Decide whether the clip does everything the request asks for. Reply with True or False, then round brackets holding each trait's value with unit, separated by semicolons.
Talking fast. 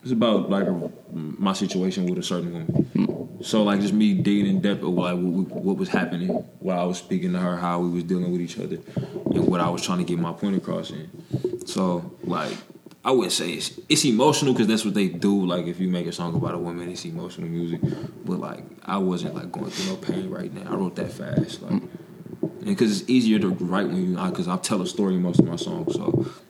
True (240 wpm)